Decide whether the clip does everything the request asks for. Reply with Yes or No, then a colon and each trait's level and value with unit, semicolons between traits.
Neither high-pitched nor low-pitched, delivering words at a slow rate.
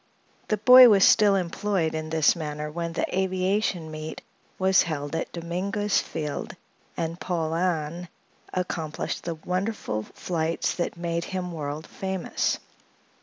Yes: medium, 170 Hz; slow, 125 wpm